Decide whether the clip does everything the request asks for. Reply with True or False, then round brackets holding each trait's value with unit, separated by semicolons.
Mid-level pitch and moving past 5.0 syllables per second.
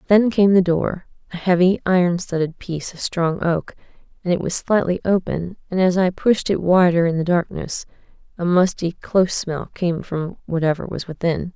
False (175 Hz; 4.9 syllables/s)